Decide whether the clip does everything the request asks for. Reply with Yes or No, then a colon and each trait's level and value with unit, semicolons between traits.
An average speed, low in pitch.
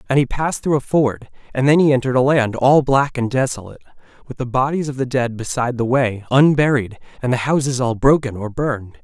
No: fast, 220 wpm; low, 130 Hz